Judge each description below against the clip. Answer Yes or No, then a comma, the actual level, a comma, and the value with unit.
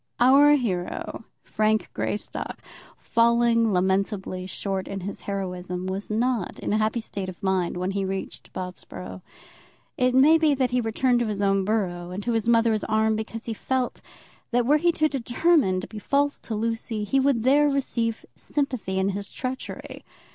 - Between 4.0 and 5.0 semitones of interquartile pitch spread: Yes, average, 4.6 semitones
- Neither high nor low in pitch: No, high, 220 Hz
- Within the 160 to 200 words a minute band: Yes, average, 170 wpm